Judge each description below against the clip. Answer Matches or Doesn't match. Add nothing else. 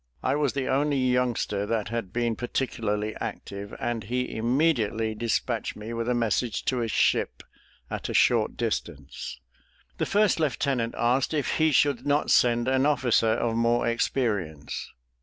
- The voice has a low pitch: Matches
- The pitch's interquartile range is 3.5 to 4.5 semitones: Doesn't match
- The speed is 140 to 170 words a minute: Matches